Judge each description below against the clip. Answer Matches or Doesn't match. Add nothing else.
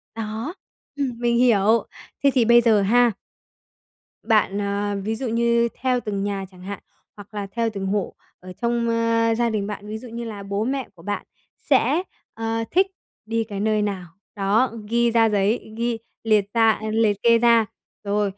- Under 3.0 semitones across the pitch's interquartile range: Matches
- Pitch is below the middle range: Doesn't match